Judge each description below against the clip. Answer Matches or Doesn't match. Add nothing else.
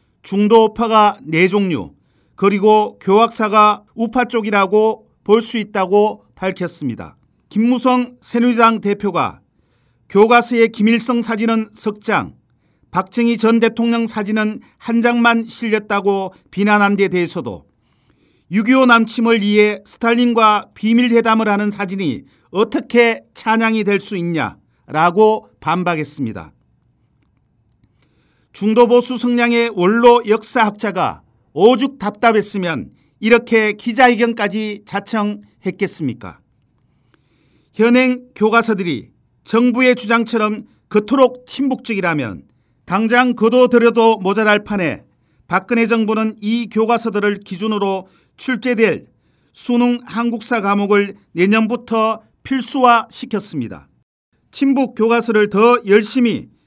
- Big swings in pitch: Doesn't match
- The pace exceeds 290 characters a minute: Doesn't match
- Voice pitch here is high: Matches